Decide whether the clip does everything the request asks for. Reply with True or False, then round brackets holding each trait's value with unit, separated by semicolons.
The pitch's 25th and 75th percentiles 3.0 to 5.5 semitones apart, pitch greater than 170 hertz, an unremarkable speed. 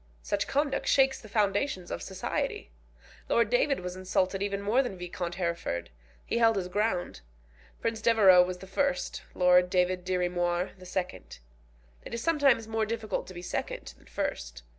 True (4.1 semitones; 190 Hz; 165 wpm)